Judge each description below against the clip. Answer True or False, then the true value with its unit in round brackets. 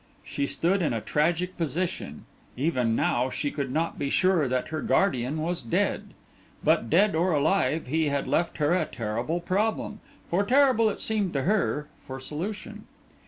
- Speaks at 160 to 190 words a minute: True (165 wpm)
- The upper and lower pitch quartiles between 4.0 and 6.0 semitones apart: True (5.1 semitones)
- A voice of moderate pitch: True (160 Hz)